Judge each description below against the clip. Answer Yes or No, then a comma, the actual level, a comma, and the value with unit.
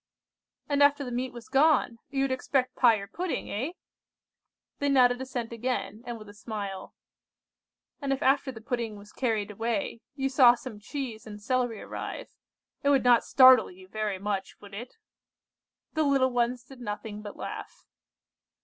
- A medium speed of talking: Yes, average, 165 wpm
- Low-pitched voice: No, high, 245 Hz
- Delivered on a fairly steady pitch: No, average, 3.9 semitones